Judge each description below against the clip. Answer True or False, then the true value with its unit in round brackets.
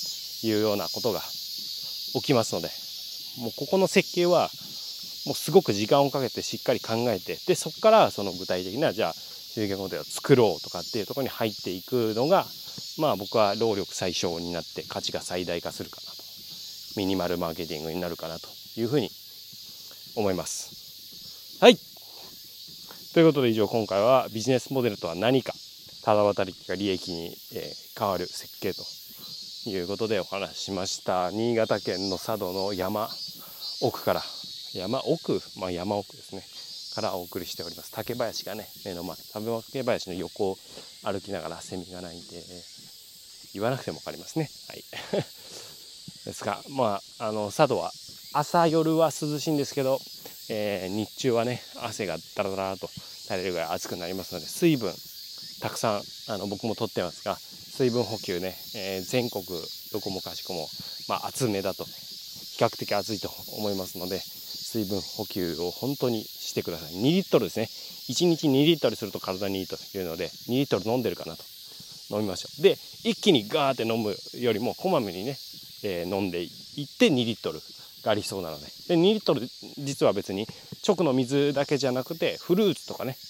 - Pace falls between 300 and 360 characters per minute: True (335 characters per minute)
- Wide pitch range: True (6.8 semitones)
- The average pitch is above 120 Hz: False (110 Hz)